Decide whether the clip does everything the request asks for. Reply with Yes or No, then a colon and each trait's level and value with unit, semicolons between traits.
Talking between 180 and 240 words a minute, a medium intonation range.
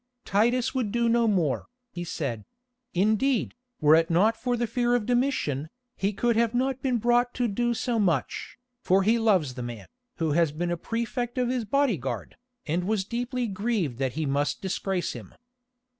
No: average, 185 wpm; wide, 6.5 semitones